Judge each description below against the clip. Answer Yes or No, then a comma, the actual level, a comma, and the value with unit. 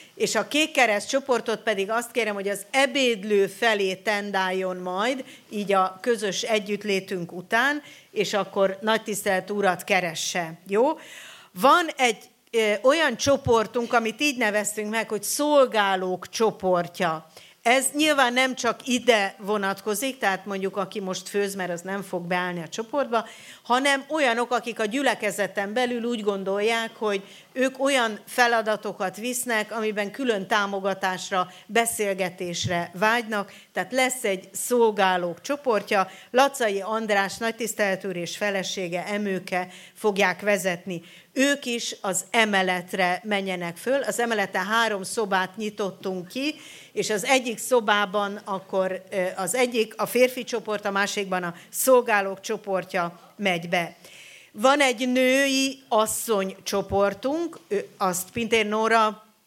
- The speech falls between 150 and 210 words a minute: No, average, 125 wpm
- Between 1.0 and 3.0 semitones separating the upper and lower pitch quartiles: No, average, 3.7 semitones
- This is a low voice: No, high, 210 Hz